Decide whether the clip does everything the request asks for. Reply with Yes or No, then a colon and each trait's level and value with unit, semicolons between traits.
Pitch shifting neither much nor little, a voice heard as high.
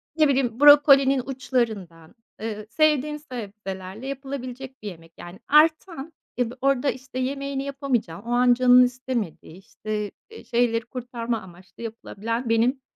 Yes: average, 3.9 semitones; very high, 250 Hz